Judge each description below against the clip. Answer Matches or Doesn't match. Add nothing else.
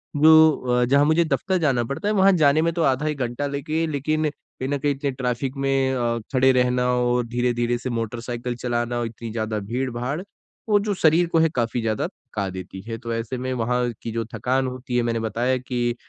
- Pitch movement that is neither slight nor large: Matches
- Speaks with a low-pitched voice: Matches